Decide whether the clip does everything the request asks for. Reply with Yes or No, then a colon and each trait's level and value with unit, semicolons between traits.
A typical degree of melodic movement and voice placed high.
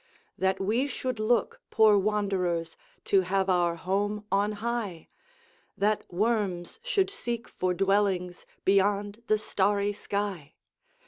No: narrow, 2.2 semitones; high, 200 Hz